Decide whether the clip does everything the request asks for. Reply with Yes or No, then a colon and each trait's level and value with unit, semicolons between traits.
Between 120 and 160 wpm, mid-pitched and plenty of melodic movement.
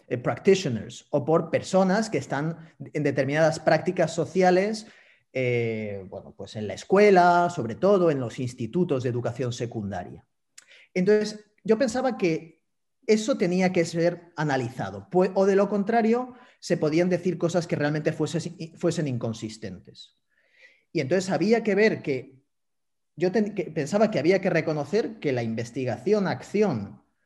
Yes: average, 145 wpm; medium, 165 Hz; wide, 6.2 semitones